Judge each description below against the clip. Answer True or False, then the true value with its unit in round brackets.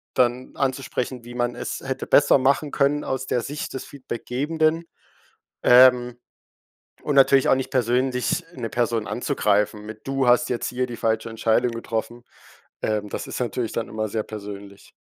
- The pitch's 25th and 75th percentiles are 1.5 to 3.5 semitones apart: True (2.8 semitones)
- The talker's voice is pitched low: True (125 Hz)